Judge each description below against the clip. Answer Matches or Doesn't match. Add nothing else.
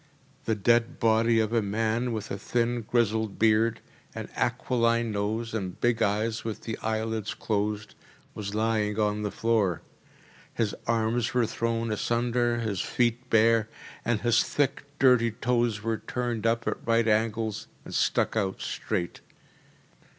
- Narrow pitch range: Matches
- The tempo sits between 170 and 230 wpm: Doesn't match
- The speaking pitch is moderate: Doesn't match